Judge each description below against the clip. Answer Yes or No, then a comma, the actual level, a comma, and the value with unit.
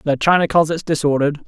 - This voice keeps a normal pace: Yes, average, 165 wpm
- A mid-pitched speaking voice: Yes, medium, 155 Hz